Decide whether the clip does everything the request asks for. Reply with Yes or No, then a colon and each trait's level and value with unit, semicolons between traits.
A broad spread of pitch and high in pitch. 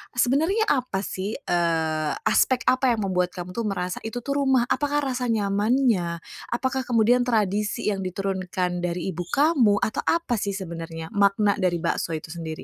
Yes: wide, 5.8 semitones; high, 205 Hz